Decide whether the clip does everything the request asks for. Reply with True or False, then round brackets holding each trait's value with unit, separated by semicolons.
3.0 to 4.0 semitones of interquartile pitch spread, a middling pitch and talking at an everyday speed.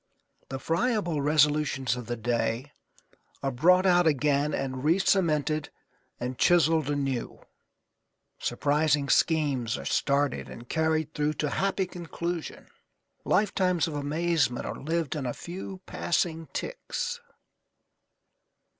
False (3.7 semitones; 150 Hz; 110 wpm)